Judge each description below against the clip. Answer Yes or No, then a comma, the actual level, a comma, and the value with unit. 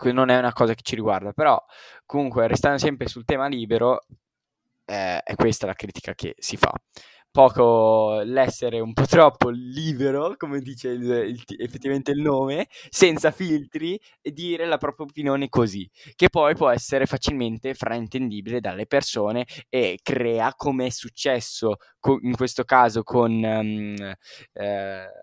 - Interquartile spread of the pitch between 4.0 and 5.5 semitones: No, average, 3.3 semitones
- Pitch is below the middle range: Yes, low, 130 Hz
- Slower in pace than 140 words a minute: No, average, 145 wpm